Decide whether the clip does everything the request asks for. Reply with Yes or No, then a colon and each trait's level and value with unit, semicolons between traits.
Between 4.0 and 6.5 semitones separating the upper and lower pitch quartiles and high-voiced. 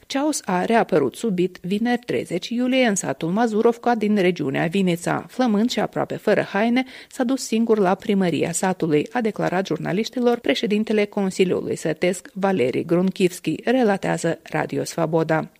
Yes: average, 4.9 semitones; high, 200 Hz